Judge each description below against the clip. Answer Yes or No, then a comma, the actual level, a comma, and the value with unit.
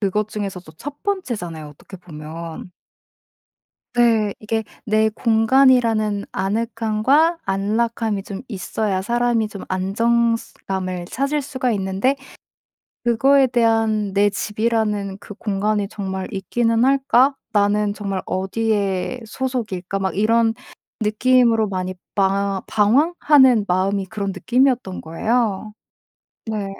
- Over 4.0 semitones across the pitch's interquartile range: No, average, 3.3 semitones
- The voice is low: No, high, 215 Hz